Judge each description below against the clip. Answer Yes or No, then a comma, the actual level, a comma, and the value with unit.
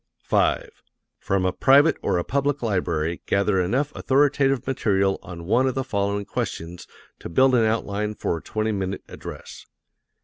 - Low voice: Yes, low, 105 Hz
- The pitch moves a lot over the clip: Yes, wide, 5.9 semitones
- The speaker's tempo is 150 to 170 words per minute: Yes, average, 160 wpm